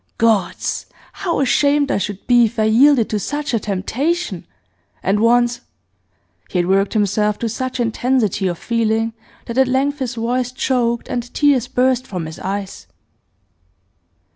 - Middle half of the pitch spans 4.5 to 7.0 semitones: No, average, 3.7 semitones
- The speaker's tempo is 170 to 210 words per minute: No, average, 155 wpm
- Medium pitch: No, high, 235 Hz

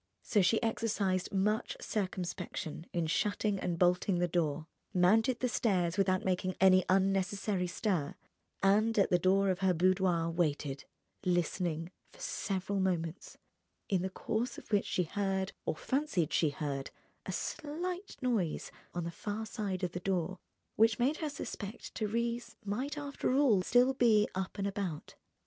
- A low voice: No, high, 190 Hz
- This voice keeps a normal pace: Yes, average, 155 wpm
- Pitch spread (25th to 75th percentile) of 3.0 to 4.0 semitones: Yes, average, 3.6 semitones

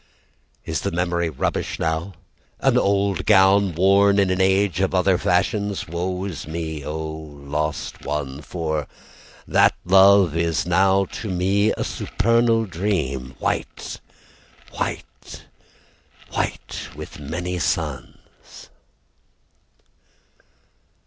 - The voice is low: Yes, very low, 90 Hz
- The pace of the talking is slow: Yes, slow, 105 wpm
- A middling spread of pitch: Yes, average, 3.7 semitones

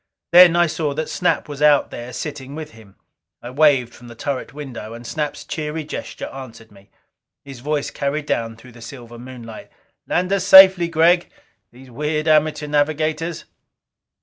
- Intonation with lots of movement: No, average, 4.3 semitones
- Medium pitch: Yes, medium, 145 Hz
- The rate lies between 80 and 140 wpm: No, average, 165 wpm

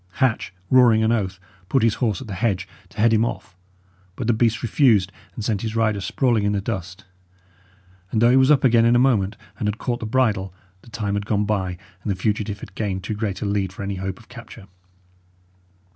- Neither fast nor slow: No, fast, 220 wpm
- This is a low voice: Yes, low, 110 Hz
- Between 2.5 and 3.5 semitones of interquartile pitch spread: Yes, average, 3.0 semitones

